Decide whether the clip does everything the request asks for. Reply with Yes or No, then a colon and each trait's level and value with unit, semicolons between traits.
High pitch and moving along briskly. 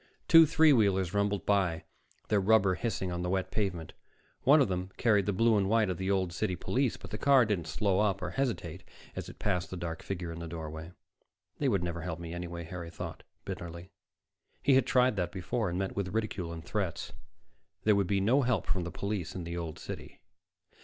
No: very low, 95 Hz; fast, 215 wpm